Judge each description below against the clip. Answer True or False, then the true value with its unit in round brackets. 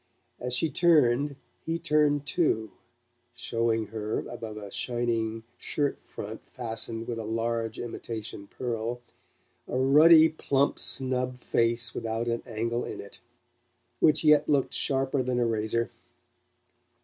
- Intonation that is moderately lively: True (3.7 semitones)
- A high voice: False (120 Hz)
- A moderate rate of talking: False (125 wpm)